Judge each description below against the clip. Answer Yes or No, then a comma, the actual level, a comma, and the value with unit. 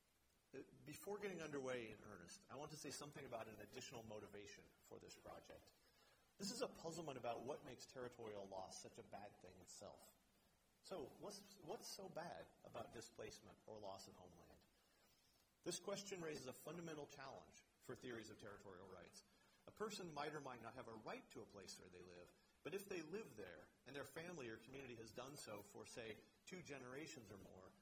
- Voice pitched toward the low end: Yes, low, 125 Hz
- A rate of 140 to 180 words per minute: No, average, 190 wpm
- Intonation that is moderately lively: No, wide, 5.8 semitones